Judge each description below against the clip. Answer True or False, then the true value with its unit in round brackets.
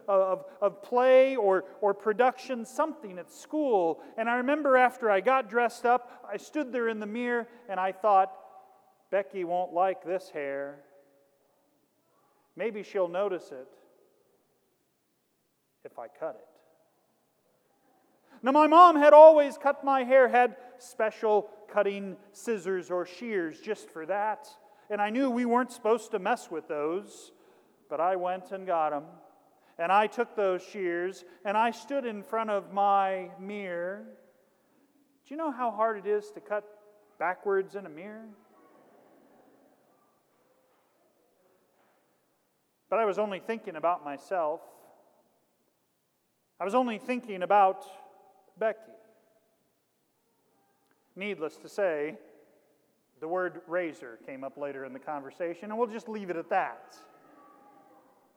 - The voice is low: False (210 Hz)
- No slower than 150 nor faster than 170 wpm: False (135 wpm)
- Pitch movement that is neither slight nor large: True (4.8 semitones)